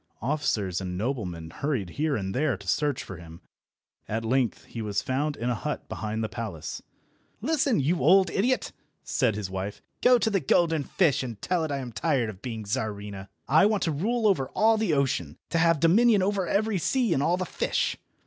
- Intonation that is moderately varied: No, wide, 9.0 semitones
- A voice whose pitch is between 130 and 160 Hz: Yes, low, 135 Hz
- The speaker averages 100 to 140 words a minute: No, fast, 205 wpm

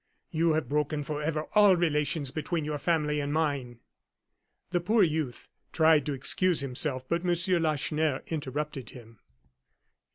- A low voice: No, medium, 150 Hz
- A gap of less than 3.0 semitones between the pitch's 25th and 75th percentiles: Yes, narrow, 2.4 semitones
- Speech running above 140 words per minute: No, slow, 135 wpm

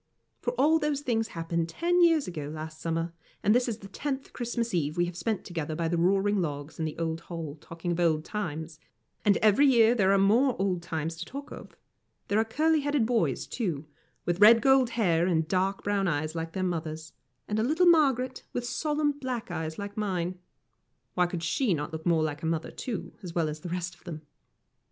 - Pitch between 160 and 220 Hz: Yes, medium, 185 Hz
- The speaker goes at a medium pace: No, fast, 210 wpm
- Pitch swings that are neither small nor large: No, wide, 6.5 semitones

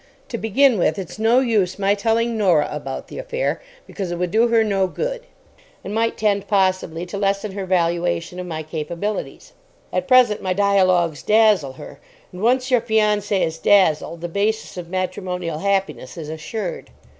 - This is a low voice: No, high, 195 Hz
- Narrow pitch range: No, average, 4.1 semitones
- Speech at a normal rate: Yes, average, 170 wpm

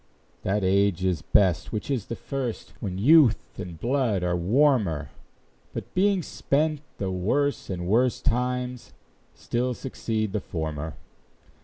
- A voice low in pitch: Yes, low, 110 Hz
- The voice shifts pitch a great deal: Yes, wide, 5.9 semitones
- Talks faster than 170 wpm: No, slow, 135 wpm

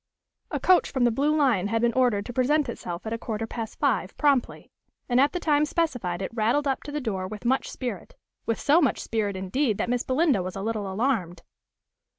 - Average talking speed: No, fast, 215 wpm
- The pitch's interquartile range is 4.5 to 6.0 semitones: Yes, average, 5.1 semitones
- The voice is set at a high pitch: Yes, high, 240 Hz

